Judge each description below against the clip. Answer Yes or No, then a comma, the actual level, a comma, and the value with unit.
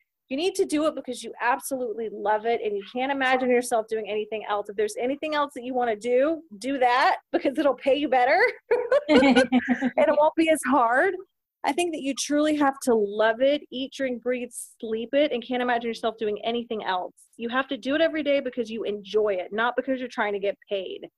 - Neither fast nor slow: No, fast, 225 wpm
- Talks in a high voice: Yes, very high, 250 Hz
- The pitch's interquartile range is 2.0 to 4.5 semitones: Yes, average, 4.0 semitones